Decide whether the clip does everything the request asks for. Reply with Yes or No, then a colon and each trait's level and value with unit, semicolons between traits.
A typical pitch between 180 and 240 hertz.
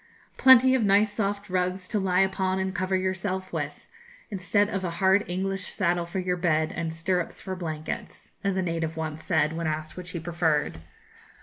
Yes: medium, 185 Hz